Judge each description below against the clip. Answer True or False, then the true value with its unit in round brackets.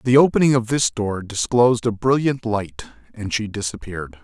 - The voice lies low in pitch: True (110 Hz)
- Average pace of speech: True (170 wpm)